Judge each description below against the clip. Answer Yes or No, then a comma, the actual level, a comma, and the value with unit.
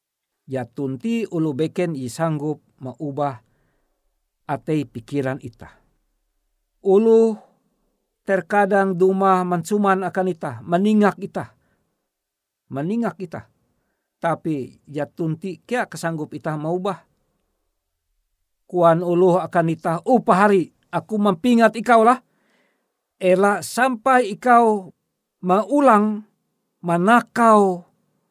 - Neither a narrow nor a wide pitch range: No, wide, 6.1 semitones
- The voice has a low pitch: No, medium, 180 Hz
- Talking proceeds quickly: No, average, 90 wpm